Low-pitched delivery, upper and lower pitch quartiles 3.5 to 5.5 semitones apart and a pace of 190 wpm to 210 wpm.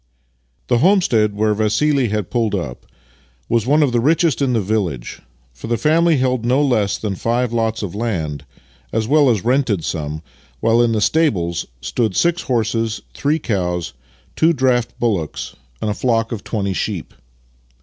No: low, 115 Hz; average, 4.1 semitones; average, 170 wpm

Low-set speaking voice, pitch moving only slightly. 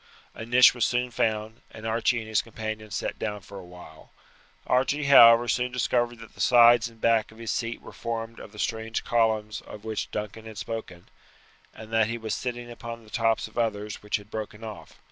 Yes: low, 115 Hz; narrow, 1.6 semitones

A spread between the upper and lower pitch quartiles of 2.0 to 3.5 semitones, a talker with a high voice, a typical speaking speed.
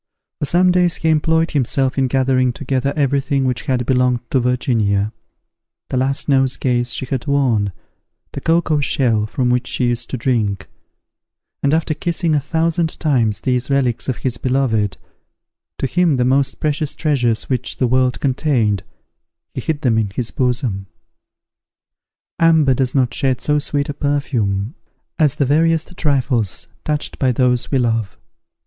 No: average, 3.0 semitones; low, 130 Hz; average, 155 wpm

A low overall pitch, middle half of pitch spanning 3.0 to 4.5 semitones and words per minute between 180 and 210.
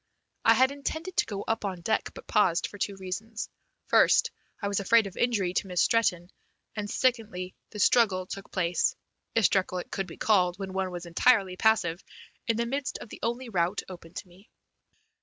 No: high, 200 Hz; average, 3.7 semitones; average, 195 wpm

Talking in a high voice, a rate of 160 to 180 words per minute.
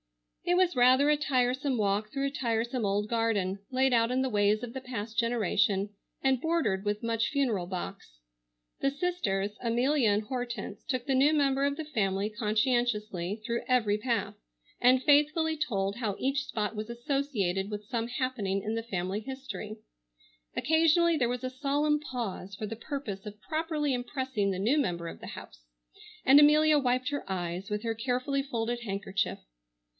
Yes: high, 240 Hz; average, 170 wpm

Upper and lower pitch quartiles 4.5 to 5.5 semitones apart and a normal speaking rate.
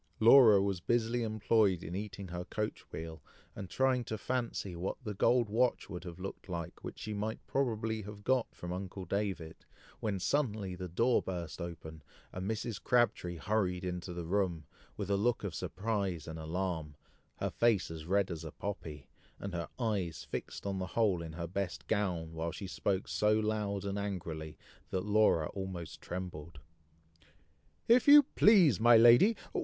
No: average, 3.9 semitones; average, 170 wpm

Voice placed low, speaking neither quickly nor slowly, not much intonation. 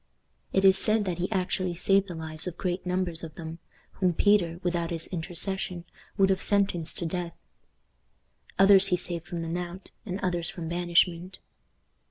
No: medium, 180 Hz; average, 170 wpm; narrow, 2.1 semitones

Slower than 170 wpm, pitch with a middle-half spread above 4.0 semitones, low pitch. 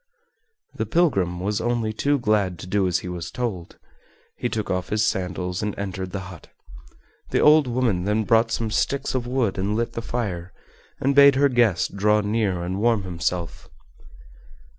No: average, 175 wpm; average, 4.5 semitones; low, 105 Hz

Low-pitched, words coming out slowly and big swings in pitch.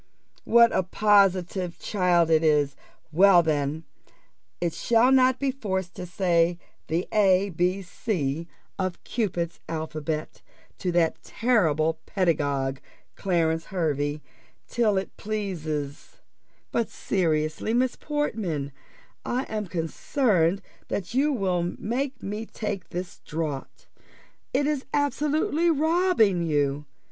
No: medium, 185 Hz; slow, 115 wpm; wide, 5.8 semitones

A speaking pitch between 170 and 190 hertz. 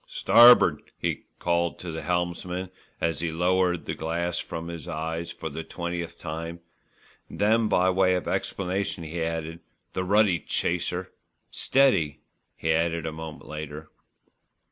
No: very low, 85 Hz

